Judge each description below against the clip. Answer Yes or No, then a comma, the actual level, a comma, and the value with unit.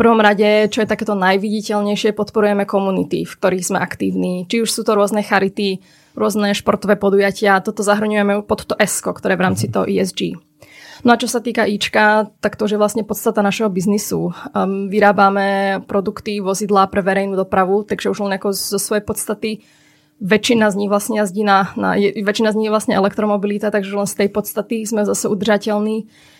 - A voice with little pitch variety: Yes, narrow, 1.5 semitones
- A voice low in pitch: No, high, 205 Hz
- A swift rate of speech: Yes, fast, 185 wpm